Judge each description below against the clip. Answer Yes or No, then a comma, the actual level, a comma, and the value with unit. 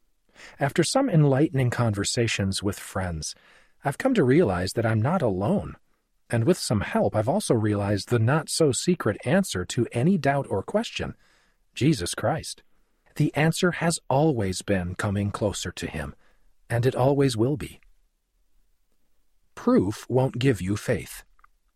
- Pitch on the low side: Yes, low, 125 Hz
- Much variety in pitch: Yes, wide, 7.3 semitones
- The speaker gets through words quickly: No, average, 145 wpm